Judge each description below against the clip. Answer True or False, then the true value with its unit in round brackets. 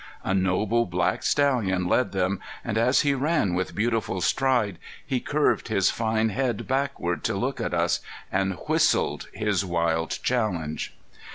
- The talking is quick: False (150 wpm)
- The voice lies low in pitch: True (105 Hz)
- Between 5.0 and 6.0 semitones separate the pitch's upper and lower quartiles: True (5.3 semitones)